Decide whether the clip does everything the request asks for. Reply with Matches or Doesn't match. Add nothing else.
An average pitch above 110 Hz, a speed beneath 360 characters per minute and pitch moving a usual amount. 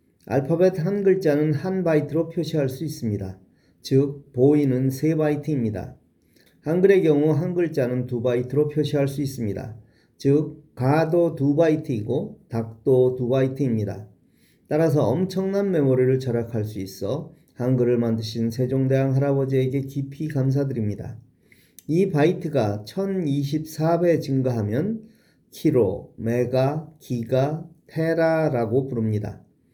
Matches